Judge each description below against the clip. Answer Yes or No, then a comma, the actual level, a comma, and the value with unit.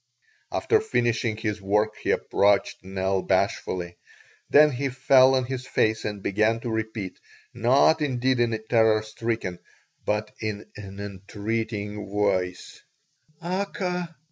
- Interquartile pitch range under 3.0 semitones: No, average, 3.7 semitones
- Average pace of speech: No, slow, 125 wpm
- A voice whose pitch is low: Yes, low, 110 Hz